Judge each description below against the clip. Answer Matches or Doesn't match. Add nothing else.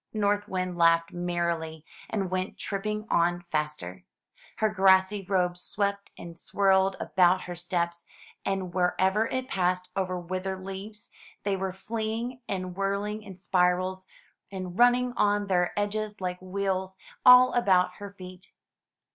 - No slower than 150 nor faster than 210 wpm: Doesn't match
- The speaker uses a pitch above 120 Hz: Matches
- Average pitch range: Doesn't match